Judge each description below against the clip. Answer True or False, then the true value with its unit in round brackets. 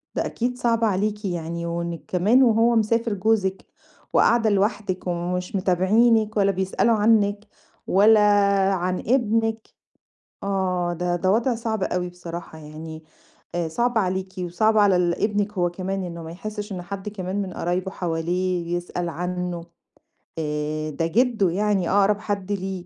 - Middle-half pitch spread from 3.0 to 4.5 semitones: True (3.4 semitones)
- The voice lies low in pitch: False (190 Hz)